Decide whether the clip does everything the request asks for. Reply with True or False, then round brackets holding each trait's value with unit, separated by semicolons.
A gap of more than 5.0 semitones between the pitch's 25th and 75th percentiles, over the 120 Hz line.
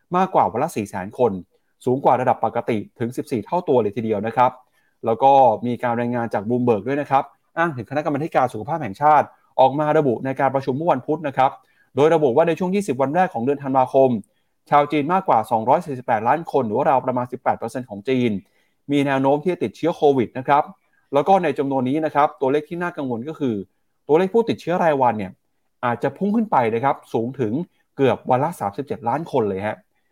False (3.9 semitones; 135 Hz)